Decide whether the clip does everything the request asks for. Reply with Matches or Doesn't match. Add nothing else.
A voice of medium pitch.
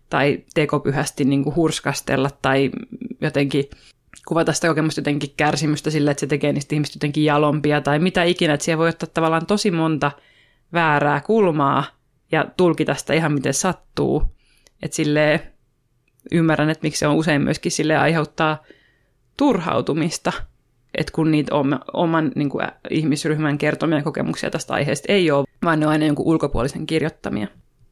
Matches